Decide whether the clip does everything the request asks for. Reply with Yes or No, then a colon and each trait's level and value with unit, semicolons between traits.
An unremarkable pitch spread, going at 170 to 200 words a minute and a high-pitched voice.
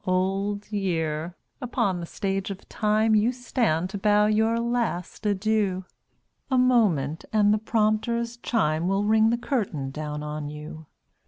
No: average, 4.4 semitones; average, 145 wpm; high, 205 Hz